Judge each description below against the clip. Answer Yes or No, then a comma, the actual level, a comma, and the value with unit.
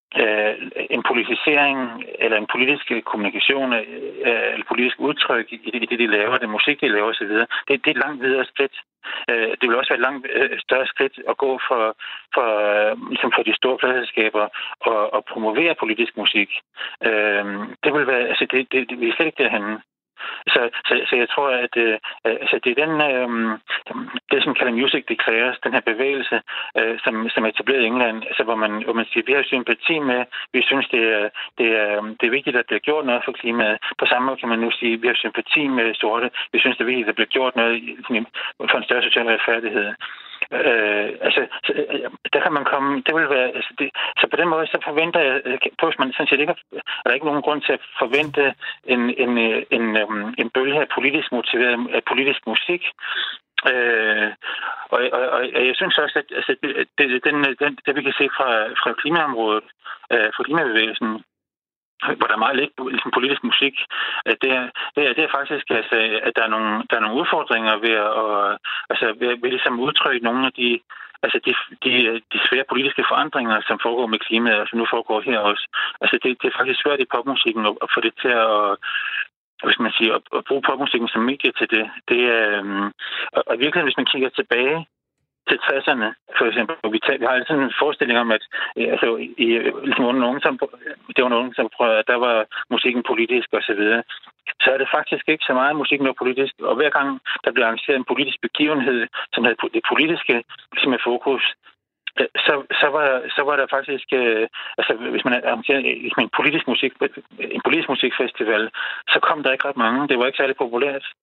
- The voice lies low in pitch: Yes, low, 125 Hz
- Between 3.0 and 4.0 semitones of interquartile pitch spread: No, average, 4.5 semitones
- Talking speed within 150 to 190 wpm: No, average, 205 wpm